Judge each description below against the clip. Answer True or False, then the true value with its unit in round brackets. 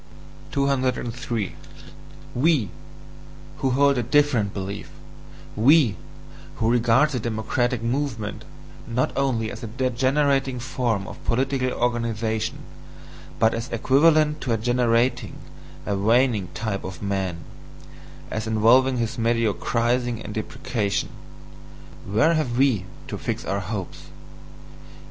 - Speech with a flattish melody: False (3.2 semitones)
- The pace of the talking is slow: True (110 wpm)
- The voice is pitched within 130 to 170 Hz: False (120 Hz)